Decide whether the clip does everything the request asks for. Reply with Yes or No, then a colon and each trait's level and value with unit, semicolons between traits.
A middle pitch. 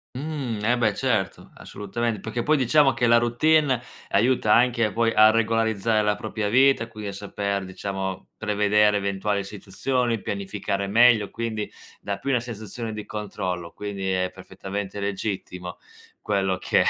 No: low, 105 Hz